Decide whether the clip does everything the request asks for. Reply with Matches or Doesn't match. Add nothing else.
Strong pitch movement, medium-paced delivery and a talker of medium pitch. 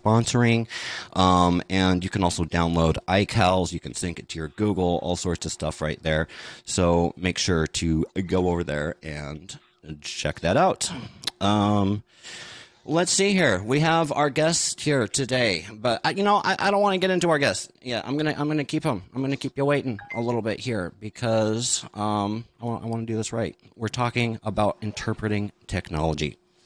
Doesn't match